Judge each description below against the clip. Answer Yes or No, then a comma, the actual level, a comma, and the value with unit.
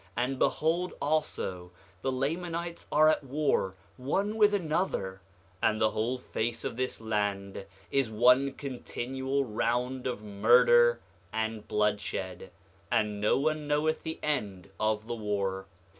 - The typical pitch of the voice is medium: No, low, 120 Hz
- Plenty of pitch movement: Yes, wide, 5.7 semitones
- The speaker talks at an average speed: No, slow, 130 wpm